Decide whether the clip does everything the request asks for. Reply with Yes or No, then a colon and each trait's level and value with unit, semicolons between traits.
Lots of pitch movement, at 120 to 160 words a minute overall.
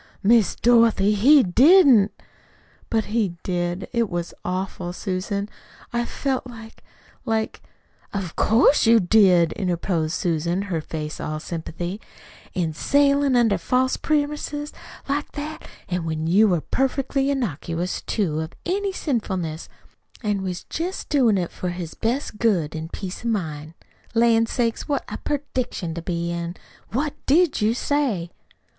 Yes: wide, 6.6 semitones; average, 140 wpm